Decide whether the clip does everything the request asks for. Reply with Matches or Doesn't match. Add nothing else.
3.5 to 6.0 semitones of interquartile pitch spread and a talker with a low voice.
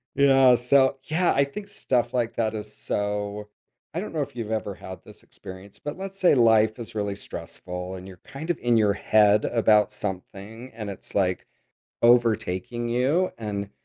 Matches